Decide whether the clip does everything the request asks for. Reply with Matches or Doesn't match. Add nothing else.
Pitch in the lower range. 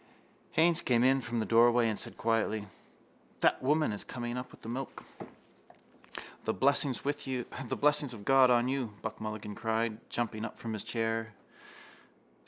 Matches